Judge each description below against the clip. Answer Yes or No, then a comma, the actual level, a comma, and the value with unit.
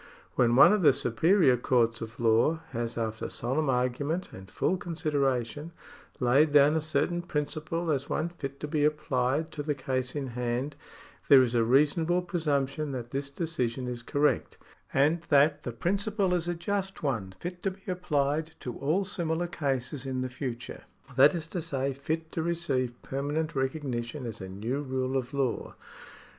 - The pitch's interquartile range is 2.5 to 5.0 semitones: Yes, average, 4.3 semitones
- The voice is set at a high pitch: No, medium, 140 Hz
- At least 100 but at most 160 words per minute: No, average, 170 wpm